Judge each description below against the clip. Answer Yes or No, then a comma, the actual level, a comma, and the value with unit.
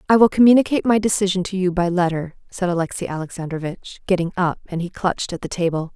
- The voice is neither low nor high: Yes, medium, 180 Hz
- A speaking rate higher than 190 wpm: Yes, average, 200 wpm